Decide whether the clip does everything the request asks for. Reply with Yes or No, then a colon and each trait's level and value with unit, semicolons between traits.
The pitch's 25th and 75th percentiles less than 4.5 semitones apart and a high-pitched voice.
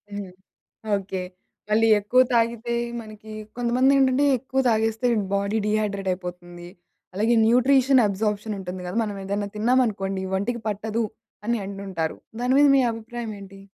Yes: average, 3.2 semitones; high, 215 Hz